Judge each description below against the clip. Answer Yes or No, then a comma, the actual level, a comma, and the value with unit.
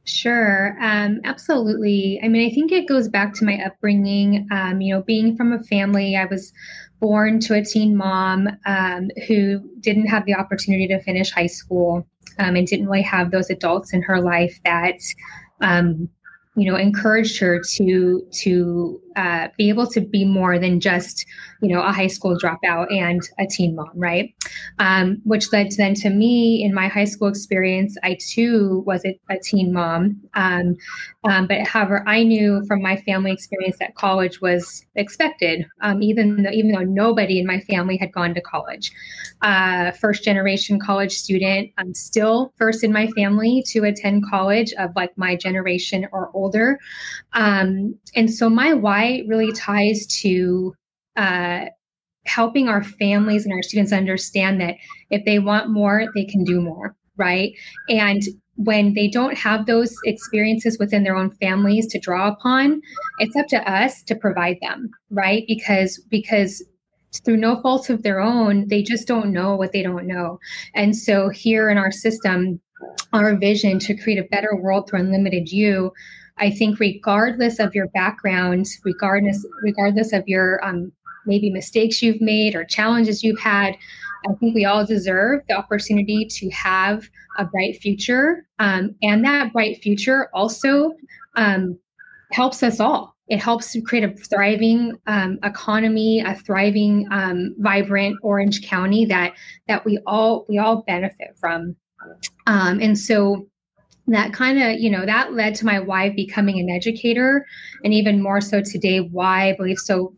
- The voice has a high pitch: Yes, high, 200 Hz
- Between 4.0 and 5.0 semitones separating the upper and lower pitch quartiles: No, narrow, 2.4 semitones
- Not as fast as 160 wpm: No, average, 165 wpm